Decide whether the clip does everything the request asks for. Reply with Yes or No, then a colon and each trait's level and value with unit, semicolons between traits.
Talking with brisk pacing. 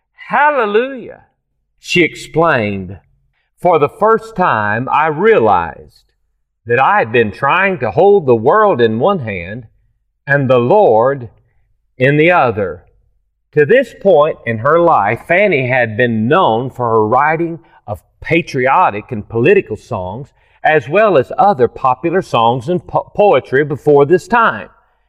No: slow, 135 wpm